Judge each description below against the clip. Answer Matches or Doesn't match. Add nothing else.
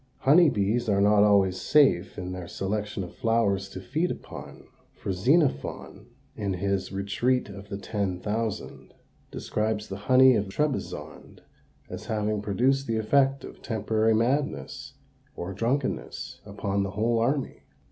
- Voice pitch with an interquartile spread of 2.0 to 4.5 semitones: Matches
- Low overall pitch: Matches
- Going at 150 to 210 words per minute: Doesn't match